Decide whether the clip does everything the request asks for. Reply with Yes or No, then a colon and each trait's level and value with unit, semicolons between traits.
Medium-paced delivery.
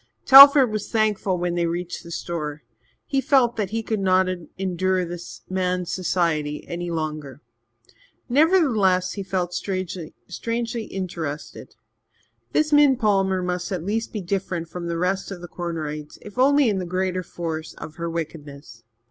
Yes: average, 150 wpm